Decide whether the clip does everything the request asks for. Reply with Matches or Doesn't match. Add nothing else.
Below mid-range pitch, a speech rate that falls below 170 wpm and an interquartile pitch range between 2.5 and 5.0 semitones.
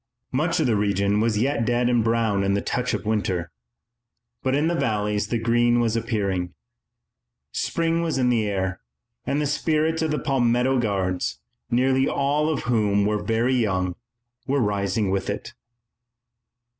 Matches